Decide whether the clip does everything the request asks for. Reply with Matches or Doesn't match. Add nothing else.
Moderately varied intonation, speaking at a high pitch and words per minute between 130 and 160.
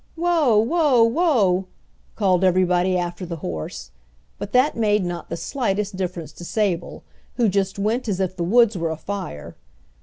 Matches